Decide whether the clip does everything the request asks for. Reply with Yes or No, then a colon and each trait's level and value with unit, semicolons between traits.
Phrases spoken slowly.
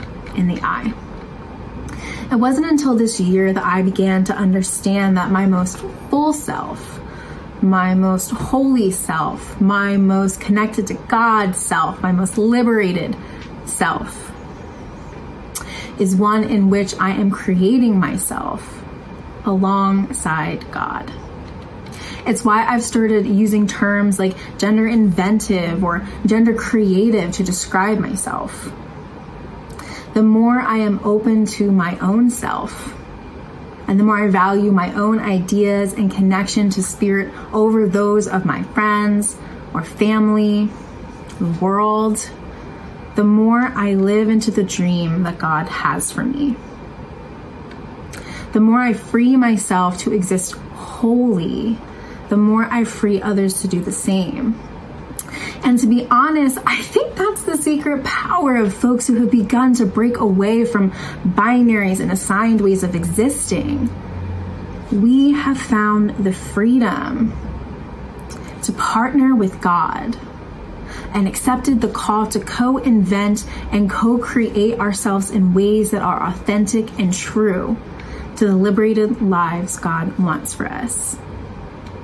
Yes: slow, 130 wpm